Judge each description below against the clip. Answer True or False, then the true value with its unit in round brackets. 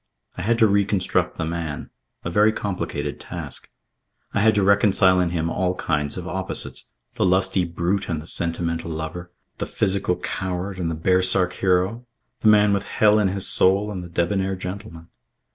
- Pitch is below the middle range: True (95 Hz)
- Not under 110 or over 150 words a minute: False (175 wpm)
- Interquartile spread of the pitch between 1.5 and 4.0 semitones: True (2.8 semitones)